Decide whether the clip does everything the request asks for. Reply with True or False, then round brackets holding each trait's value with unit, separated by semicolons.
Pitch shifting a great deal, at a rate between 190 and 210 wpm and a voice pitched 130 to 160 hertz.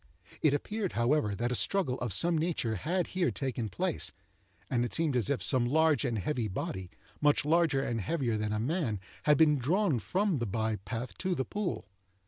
True (6.1 semitones; 195 wpm; 135 Hz)